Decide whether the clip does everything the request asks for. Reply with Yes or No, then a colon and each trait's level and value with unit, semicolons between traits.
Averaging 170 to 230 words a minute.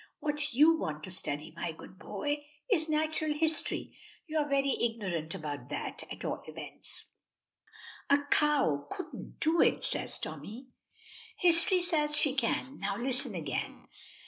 No: average, 145 wpm